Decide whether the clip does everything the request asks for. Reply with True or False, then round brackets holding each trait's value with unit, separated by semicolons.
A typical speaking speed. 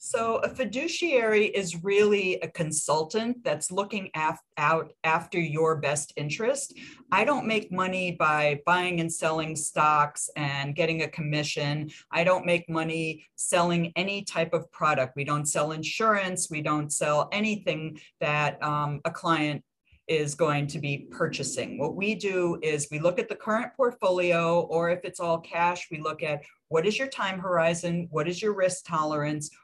True (165 wpm)